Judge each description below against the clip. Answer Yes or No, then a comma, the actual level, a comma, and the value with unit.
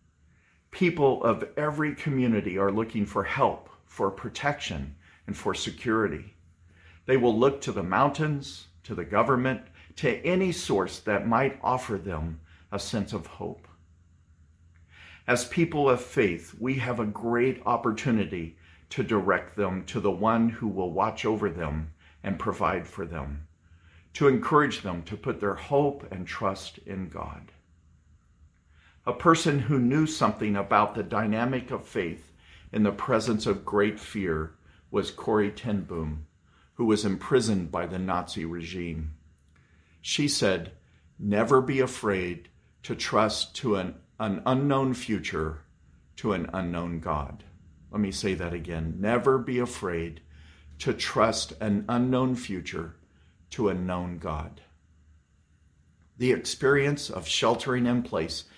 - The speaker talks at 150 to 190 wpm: No, slow, 135 wpm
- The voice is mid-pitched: No, very low, 95 Hz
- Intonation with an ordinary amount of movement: No, wide, 6.5 semitones